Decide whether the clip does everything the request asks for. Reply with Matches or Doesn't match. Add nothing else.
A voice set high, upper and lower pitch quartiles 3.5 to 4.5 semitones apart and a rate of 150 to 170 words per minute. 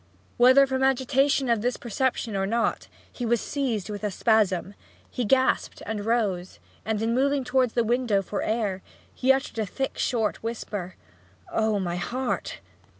Matches